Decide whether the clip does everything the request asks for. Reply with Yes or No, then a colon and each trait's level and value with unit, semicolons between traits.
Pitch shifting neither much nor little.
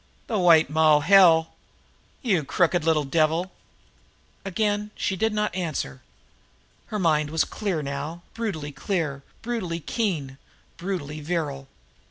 Yes: average, 4.4 semitones